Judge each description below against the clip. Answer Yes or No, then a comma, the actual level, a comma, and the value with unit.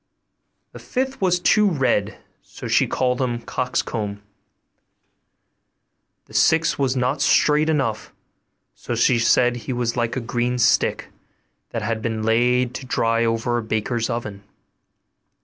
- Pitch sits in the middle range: No, low, 120 Hz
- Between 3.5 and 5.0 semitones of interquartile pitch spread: No, narrow, 2.5 semitones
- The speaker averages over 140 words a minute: No, slow, 135 wpm